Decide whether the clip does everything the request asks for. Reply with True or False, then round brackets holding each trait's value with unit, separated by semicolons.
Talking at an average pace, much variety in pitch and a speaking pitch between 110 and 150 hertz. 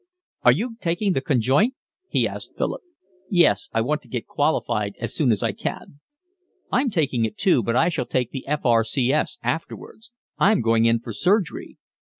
True (185 wpm; 7.1 semitones; 140 Hz)